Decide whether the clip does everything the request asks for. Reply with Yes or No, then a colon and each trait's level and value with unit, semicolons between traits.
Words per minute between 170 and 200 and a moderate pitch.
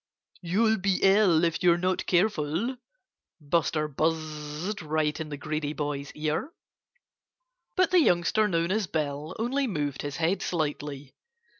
No: slow, 135 wpm; medium, 165 Hz